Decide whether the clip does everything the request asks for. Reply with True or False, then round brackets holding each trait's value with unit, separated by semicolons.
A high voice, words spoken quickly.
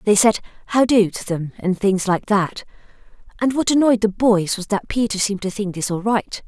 True (205 Hz; 220 wpm)